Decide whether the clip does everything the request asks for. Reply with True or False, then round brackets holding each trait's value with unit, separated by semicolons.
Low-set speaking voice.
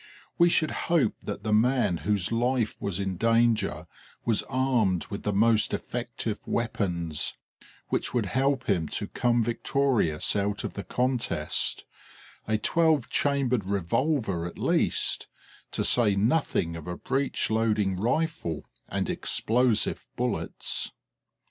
True (115 Hz)